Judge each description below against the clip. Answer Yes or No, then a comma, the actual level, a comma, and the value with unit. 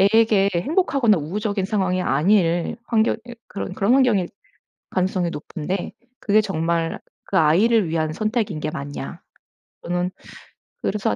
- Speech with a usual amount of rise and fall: Yes, average, 4.4 semitones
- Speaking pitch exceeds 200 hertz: No, high, 190 Hz